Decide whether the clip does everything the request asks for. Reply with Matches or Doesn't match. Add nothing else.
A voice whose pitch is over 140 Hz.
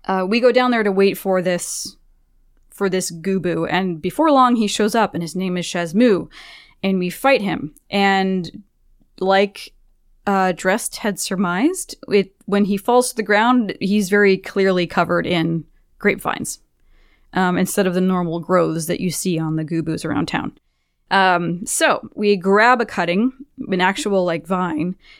Matches